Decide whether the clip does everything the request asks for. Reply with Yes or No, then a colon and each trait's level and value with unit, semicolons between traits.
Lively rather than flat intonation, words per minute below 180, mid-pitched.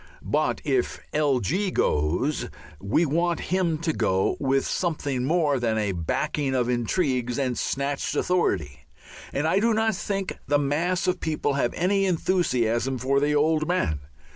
Yes: wide, 5.8 semitones; average, 155 wpm; medium, 145 Hz